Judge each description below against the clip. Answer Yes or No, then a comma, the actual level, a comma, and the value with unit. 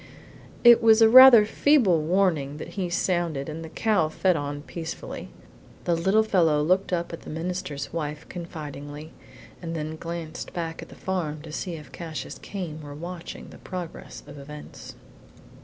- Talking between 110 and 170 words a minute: Yes, average, 165 wpm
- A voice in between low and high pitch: Yes, medium, 165 Hz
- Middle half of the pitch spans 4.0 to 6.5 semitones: No, average, 3.4 semitones